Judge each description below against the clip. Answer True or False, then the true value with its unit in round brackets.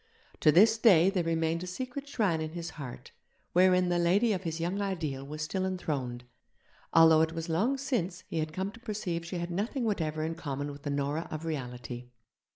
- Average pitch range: True (3.5 semitones)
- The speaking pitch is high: False (170 Hz)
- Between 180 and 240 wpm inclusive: True (200 wpm)